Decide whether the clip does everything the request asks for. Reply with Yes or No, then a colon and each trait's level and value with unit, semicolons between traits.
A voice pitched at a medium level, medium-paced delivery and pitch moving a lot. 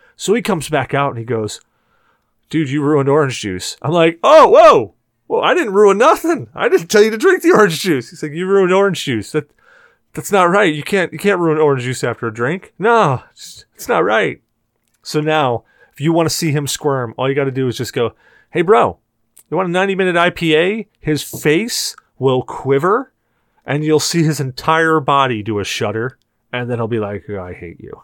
No: medium, 150 Hz; fast, 215 wpm; wide, 6.0 semitones